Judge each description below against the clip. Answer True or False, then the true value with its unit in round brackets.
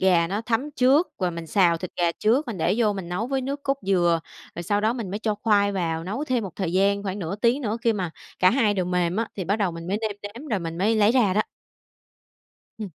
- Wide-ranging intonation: False (4.0 semitones)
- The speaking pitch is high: True (200 Hz)